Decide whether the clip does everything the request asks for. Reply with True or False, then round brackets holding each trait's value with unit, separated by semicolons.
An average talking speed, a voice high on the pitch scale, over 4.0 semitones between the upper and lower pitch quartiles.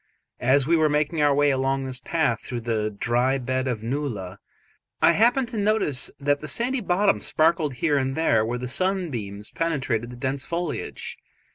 False (180 wpm; 140 Hz; 5.1 semitones)